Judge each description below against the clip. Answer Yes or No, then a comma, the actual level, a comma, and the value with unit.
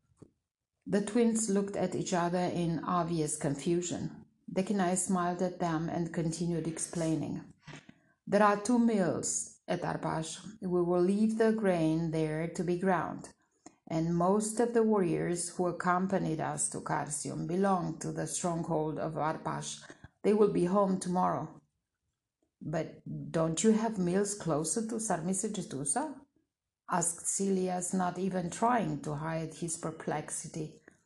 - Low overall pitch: No, medium, 180 Hz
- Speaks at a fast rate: No, slow, 135 wpm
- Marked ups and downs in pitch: No, average, 3.4 semitones